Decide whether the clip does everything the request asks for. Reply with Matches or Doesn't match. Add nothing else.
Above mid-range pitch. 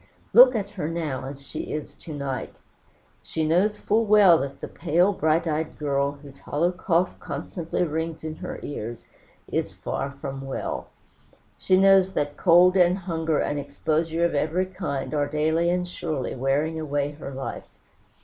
Doesn't match